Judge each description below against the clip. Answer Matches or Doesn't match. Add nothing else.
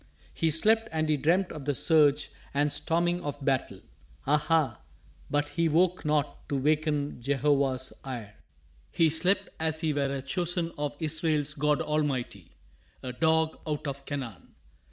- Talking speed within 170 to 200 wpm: Doesn't match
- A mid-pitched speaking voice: Matches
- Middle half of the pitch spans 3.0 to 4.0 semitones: Doesn't match